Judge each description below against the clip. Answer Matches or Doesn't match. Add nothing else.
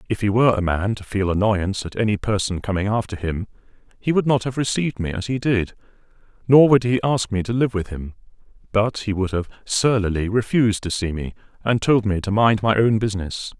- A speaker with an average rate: Doesn't match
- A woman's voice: Doesn't match